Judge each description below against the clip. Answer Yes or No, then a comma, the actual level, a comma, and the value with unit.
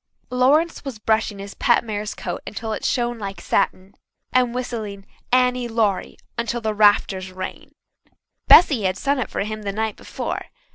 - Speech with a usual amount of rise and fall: Yes, average, 3.5 semitones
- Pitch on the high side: Yes, high, 220 Hz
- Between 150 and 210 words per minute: Yes, average, 160 wpm